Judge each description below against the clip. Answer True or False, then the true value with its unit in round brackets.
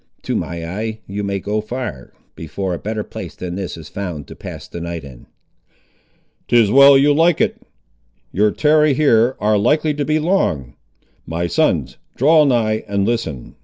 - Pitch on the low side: True (105 Hz)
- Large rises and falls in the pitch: True (7.8 semitones)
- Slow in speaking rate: False (170 wpm)